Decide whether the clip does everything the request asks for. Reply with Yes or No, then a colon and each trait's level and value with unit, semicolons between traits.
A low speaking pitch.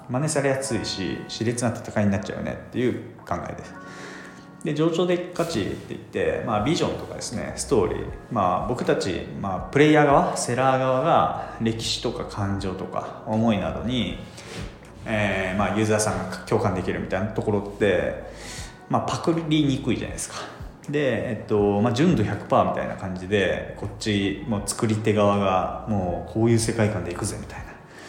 Yes: low, 110 Hz